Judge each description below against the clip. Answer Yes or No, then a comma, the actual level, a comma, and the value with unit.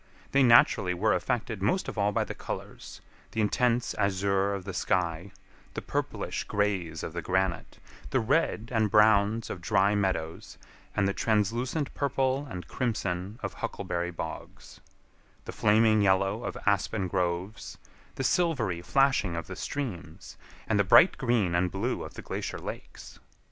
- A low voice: Yes, low, 100 Hz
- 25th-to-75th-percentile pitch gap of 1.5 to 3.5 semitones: No, average, 3.9 semitones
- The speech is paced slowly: No, average, 150 wpm